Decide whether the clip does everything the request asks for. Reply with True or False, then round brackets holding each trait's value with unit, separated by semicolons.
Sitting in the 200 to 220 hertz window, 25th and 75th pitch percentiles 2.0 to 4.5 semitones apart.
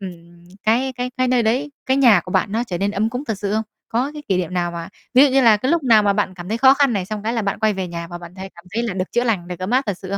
False (215 Hz; 5.1 semitones)